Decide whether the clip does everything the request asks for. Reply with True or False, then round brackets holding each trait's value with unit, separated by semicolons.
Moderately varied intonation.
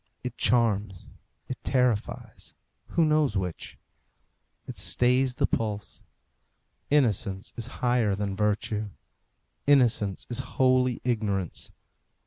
True (3.7 semitones)